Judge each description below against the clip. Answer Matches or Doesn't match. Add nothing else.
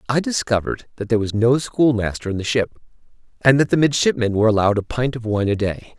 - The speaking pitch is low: Matches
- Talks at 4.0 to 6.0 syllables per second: Doesn't match